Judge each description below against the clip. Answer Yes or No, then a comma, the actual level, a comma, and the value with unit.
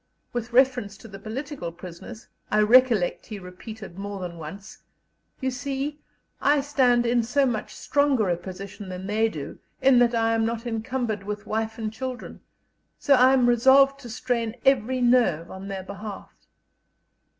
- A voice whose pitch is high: Yes, high, 225 Hz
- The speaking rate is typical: Yes, average, 160 wpm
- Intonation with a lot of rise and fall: No, average, 4.2 semitones